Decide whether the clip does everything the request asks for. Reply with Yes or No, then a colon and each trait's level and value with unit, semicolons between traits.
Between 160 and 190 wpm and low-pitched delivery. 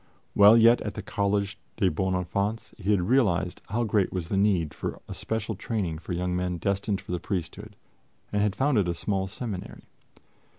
Yes: average, 185 wpm; low, 100 Hz